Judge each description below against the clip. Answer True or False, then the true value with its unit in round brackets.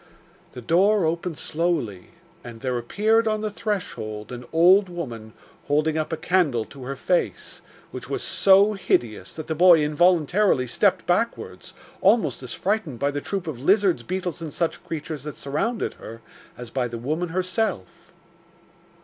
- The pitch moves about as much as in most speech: False (6.6 semitones)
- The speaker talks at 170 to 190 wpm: False (160 wpm)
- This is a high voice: False (160 Hz)